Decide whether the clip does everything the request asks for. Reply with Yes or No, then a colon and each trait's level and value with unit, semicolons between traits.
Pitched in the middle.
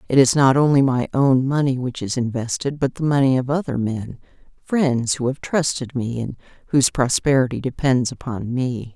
No: low, 130 Hz